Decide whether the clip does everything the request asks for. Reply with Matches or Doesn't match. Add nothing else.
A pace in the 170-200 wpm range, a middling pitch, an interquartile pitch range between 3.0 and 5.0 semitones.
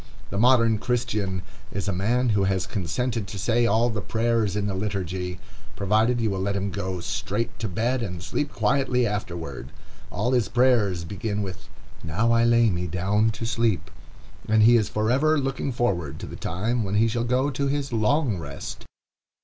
Doesn't match